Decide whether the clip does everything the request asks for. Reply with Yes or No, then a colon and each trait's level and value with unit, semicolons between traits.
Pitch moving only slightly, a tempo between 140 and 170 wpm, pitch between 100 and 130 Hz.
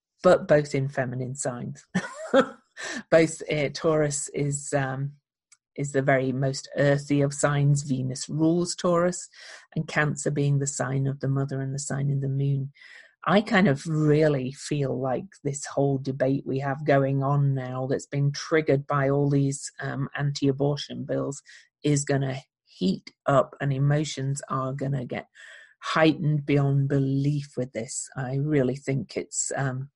No: narrow, 1.8 semitones; average, 155 wpm; medium, 140 Hz